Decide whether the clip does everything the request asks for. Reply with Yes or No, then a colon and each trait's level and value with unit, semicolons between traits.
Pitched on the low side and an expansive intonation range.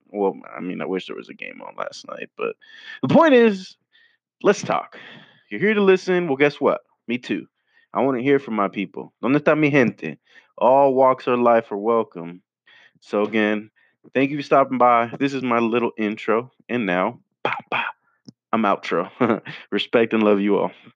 Yes: low, 125 Hz; wide, 5.7 semitones